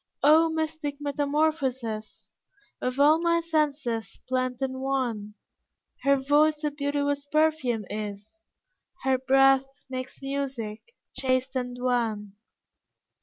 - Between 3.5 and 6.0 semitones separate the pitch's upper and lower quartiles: No, average, 2.9 semitones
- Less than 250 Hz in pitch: No, very high, 270 Hz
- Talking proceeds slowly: Yes, slow, 105 wpm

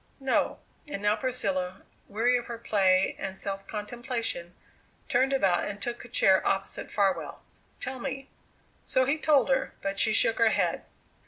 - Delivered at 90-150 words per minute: No, average, 160 wpm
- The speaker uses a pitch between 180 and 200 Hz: No, high, 220 Hz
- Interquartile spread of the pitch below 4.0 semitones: No, average, 4.4 semitones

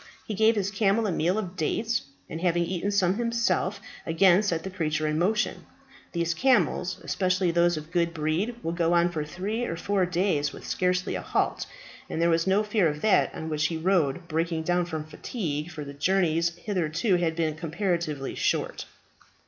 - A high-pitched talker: No, medium, 175 Hz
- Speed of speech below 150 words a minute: No, average, 190 wpm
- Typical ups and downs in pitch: Yes, average, 3.2 semitones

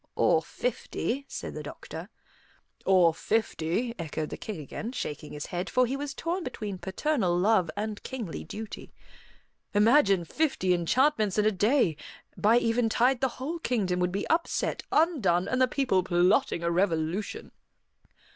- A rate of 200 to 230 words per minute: No, average, 145 wpm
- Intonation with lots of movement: Yes, wide, 6.3 semitones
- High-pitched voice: Yes, high, 215 Hz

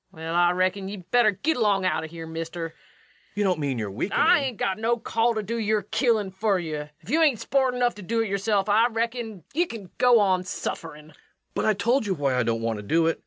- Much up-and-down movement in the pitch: Yes, wide, 5.8 semitones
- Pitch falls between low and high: No, high, 200 Hz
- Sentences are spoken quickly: Yes, fast, 260 wpm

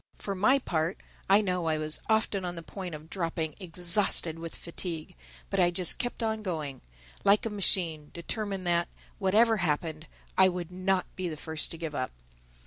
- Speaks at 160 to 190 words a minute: Yes, average, 170 wpm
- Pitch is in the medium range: Yes, medium, 175 Hz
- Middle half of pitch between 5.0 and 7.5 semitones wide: No, average, 3.5 semitones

